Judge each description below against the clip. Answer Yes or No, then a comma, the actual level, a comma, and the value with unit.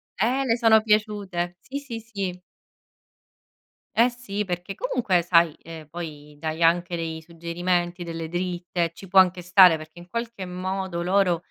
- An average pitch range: Yes, average, 3.1 semitones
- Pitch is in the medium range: Yes, medium, 180 Hz